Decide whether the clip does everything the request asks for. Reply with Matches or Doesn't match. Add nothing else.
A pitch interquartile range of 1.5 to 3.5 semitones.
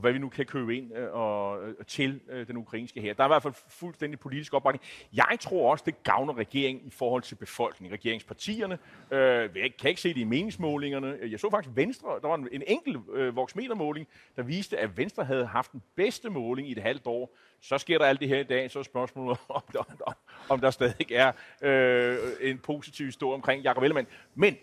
Matches